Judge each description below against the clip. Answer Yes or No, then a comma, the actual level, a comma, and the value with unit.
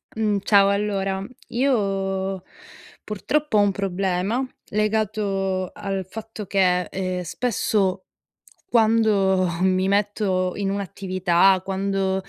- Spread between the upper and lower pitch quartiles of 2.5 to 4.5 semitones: No, narrow, 1.8 semitones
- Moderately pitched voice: No, high, 195 Hz